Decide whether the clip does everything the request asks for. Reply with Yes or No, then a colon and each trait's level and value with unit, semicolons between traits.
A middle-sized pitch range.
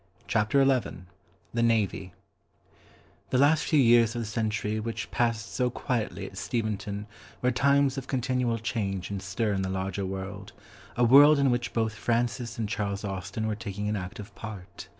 Yes: average, 3.2 semitones